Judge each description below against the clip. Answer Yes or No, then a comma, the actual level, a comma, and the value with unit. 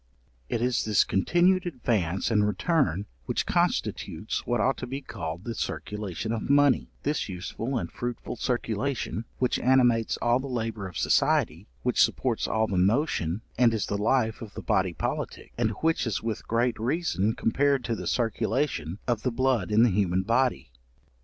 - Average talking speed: Yes, average, 170 wpm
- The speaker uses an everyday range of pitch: Yes, average, 4.0 semitones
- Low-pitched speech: Yes, low, 115 Hz